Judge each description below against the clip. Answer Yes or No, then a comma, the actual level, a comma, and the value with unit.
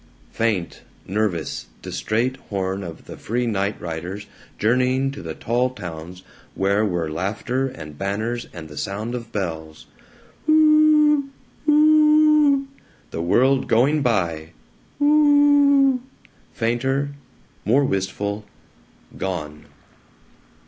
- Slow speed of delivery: Yes, slow, 105 wpm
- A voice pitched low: Yes, low, 115 Hz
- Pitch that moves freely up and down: Yes, wide, 7.5 semitones